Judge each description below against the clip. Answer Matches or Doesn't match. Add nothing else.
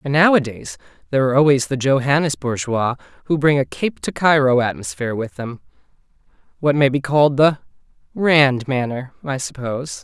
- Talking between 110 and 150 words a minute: Matches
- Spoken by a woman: Doesn't match